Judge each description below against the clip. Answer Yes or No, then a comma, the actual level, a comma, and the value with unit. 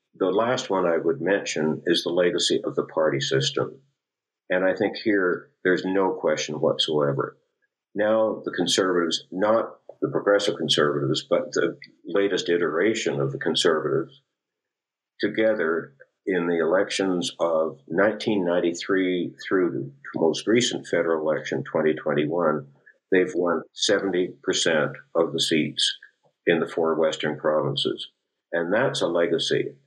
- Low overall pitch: Yes, very low, 90 Hz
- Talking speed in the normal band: No, slow, 125 wpm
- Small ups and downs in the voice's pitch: No, average, 4.8 semitones